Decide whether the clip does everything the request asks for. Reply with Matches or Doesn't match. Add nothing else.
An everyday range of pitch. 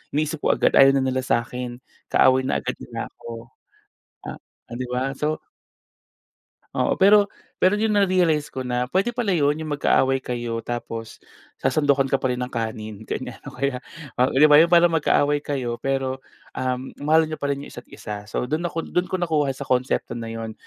Matches